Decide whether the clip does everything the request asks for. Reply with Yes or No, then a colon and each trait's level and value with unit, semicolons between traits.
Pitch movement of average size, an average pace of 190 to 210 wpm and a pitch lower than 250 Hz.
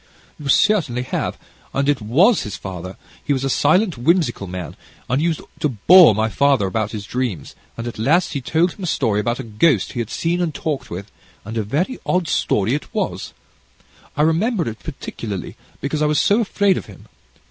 No: wide, 7.2 semitones; average, 200 wpm; low, 135 Hz